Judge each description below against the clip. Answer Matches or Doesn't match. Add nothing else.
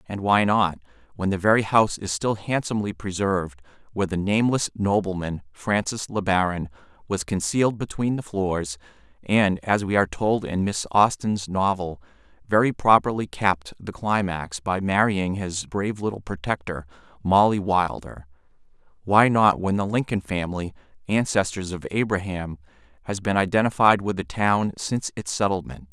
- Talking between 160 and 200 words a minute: Doesn't match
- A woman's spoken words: Doesn't match